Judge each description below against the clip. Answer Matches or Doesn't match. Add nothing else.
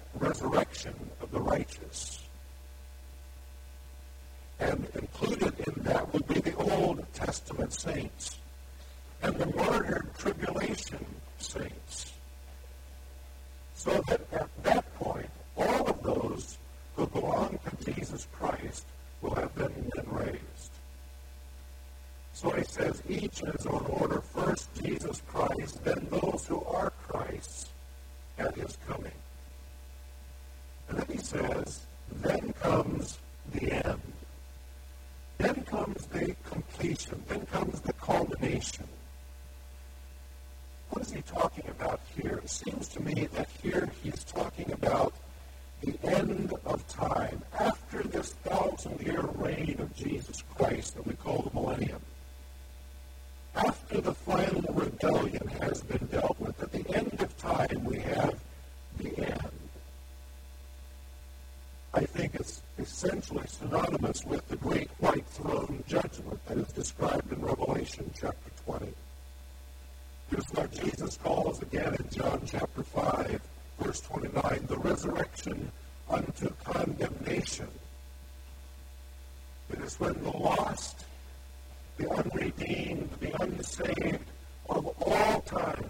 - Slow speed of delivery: Matches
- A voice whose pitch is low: Matches